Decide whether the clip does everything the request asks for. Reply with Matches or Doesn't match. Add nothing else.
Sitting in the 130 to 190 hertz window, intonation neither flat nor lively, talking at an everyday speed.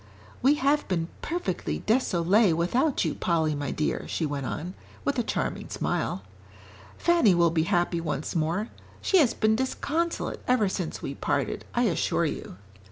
Doesn't match